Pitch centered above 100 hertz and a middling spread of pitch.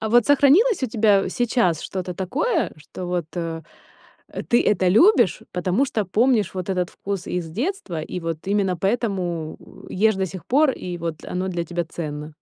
Yes: high, 190 Hz; average, 5.0 semitones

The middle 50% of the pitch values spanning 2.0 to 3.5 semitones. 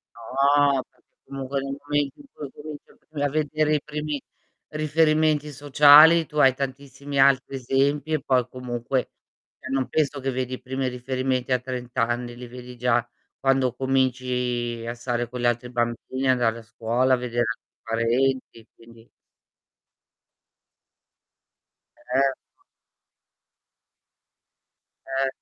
Yes: narrow, 2.4 semitones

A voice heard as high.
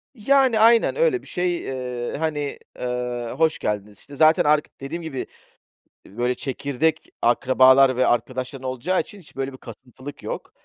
No: low, 135 Hz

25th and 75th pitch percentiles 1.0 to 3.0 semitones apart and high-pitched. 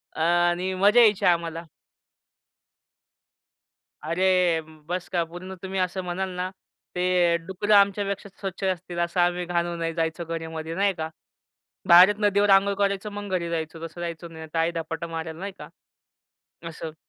No: narrow, 2.4 semitones; medium, 175 Hz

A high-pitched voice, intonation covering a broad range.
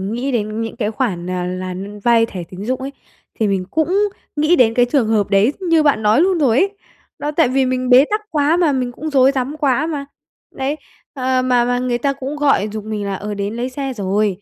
No: very high, 250 Hz; average, 4.9 semitones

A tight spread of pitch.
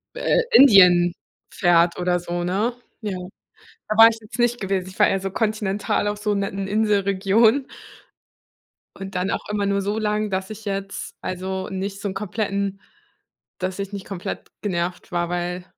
Yes: narrow, 2.2 semitones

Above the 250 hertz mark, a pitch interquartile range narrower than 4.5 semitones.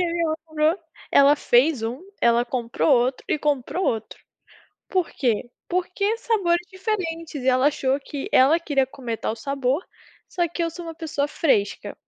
No: very high, 290 Hz; average, 4.9 semitones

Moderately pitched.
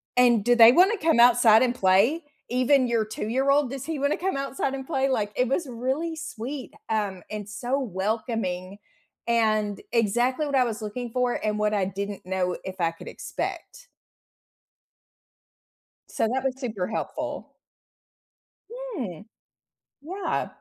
No: high, 240 Hz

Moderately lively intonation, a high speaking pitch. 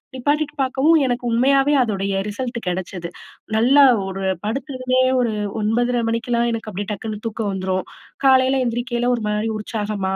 Yes: average, 3.7 semitones; high, 235 Hz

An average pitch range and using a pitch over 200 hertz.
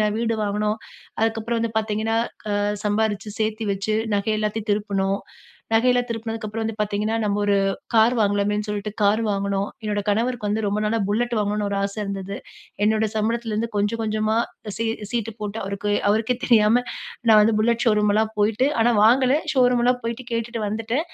No: narrow, 1.7 semitones; high, 215 Hz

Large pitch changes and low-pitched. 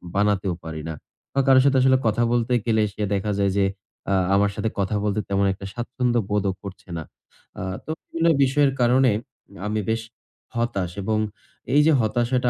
No: average, 3.9 semitones; low, 110 Hz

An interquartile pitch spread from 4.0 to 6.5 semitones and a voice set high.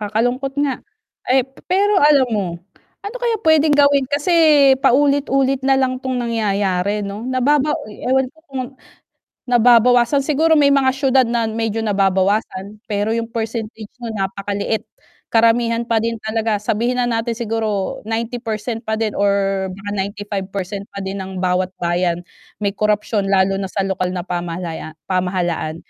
Yes: average, 4.5 semitones; high, 225 Hz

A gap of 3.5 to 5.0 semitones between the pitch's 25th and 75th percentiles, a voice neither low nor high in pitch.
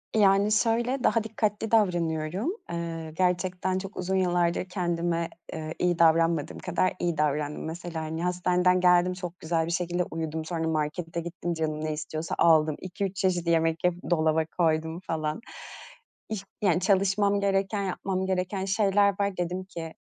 No: average, 2.7 semitones; medium, 175 Hz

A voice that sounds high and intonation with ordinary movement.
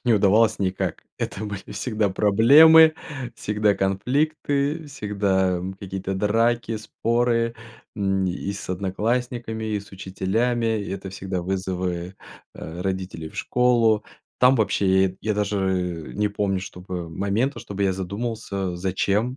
No: low, 100 Hz; average, 3.4 semitones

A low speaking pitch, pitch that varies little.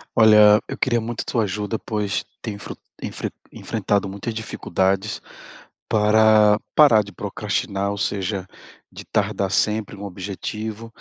Yes: low, 105 Hz; narrow, 1.7 semitones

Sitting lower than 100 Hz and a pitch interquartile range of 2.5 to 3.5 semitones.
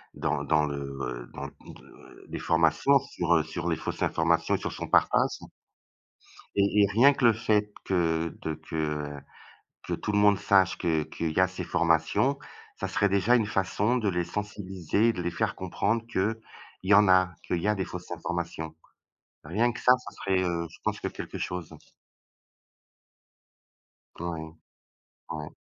No: very low, 90 Hz; average, 4.2 semitones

